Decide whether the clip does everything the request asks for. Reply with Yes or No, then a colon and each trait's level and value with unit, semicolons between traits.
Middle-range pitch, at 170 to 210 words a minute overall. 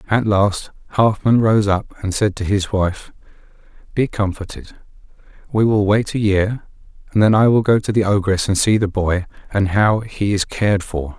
No: low, 100 Hz; average, 190 wpm